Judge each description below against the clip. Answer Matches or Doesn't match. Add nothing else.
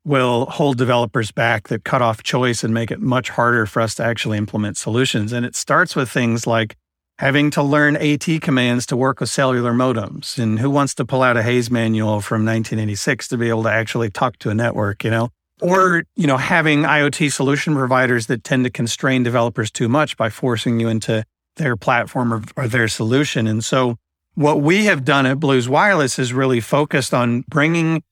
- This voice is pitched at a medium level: Doesn't match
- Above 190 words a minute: Matches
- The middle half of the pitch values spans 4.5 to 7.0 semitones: Doesn't match